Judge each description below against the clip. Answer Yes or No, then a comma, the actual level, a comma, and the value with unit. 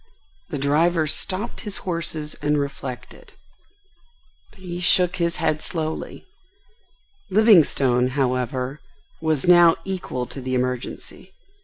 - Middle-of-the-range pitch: Yes, medium, 155 Hz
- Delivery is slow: Yes, slow, 105 wpm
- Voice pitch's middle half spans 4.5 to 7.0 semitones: Yes, average, 4.9 semitones